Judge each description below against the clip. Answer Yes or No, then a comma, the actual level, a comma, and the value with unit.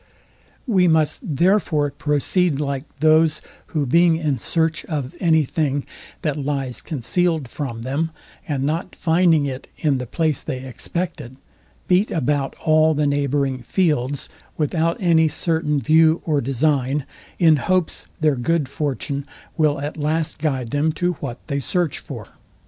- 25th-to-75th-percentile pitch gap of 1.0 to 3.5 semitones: Yes, average, 2.8 semitones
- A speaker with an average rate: Yes, average, 145 wpm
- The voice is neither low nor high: Yes, medium, 150 Hz